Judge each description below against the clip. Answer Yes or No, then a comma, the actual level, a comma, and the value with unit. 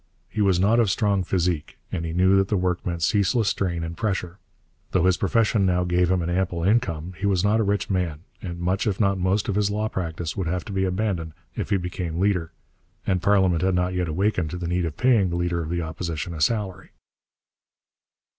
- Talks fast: Yes, fast, 220 wpm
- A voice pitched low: Yes, very low, 90 Hz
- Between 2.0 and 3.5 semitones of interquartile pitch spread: Yes, narrow, 2.5 semitones